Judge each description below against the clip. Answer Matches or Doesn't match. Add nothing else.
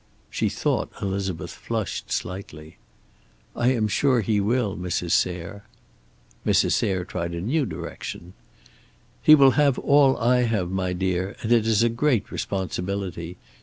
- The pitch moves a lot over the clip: Doesn't match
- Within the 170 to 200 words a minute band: Doesn't match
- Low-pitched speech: Matches